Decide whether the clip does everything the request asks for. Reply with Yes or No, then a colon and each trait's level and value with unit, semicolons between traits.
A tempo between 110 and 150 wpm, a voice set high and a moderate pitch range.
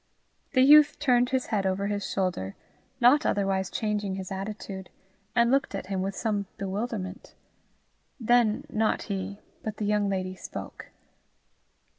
Yes: average, 140 wpm; high, 205 Hz; average, 3.6 semitones